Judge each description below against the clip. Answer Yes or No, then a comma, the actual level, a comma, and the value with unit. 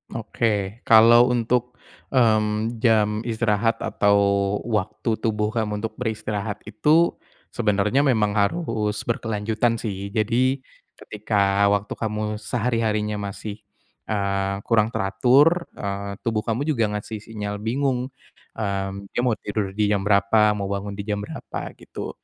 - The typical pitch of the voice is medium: No, low, 105 Hz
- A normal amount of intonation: No, narrow, 2.1 semitones